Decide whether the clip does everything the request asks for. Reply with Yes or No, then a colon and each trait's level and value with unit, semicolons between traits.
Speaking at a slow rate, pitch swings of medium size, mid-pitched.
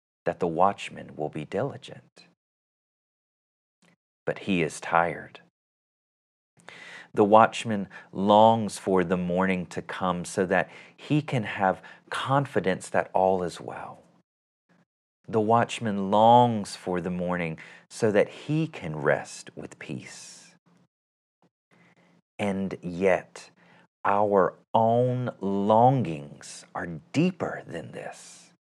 No: slow, 105 wpm; average, 4.5 semitones; very low, 95 Hz